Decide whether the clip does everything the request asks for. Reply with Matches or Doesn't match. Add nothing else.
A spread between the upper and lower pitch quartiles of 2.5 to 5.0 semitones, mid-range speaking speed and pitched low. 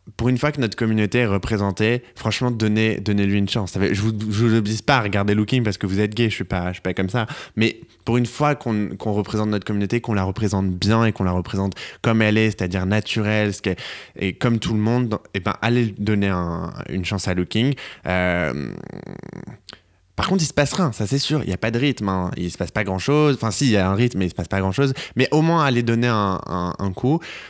Doesn't match